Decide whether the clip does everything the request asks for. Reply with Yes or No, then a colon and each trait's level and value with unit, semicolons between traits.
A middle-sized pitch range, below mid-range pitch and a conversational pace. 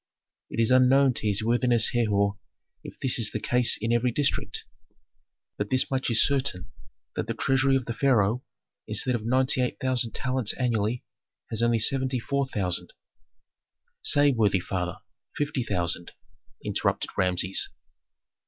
Yes: average, 3.7 semitones; low, 120 Hz; average, 150 wpm